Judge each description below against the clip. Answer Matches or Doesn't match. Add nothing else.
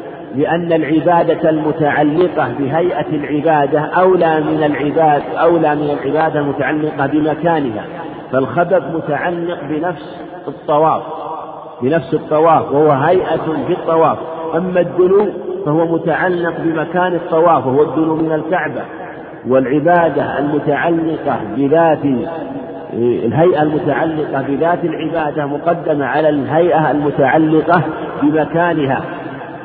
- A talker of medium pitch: Matches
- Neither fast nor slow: Matches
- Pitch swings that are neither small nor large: Doesn't match